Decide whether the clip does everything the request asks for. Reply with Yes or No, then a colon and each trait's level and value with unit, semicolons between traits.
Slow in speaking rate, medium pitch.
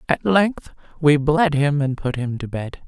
No: fast, 210 wpm; medium, 155 Hz